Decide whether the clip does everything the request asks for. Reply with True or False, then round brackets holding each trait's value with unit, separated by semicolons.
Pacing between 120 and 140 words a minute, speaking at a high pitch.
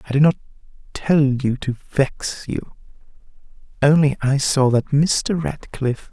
False (135 wpm; 140 Hz)